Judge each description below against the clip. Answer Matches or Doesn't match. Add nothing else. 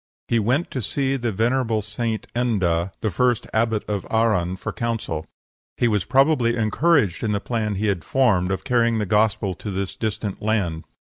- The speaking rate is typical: Matches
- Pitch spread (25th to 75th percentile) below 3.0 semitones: Doesn't match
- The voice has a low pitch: Matches